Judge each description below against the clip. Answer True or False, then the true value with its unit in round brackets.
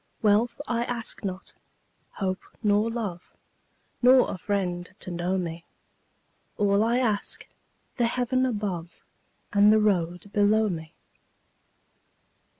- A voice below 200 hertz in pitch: False (205 Hz)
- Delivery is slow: True (115 wpm)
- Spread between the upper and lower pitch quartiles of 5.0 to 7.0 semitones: False (4.0 semitones)